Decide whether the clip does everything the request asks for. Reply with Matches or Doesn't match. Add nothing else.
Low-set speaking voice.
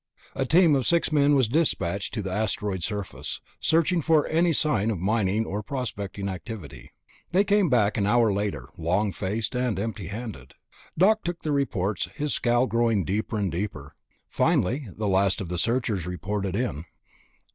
Matches